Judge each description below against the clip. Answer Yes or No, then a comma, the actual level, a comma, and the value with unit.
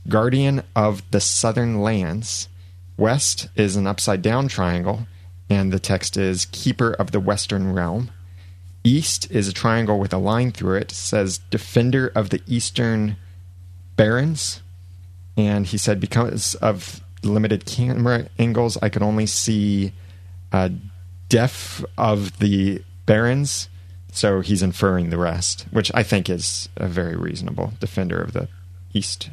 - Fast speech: No, slow, 135 wpm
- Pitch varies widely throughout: No, average, 3.5 semitones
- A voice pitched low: Yes, low, 100 Hz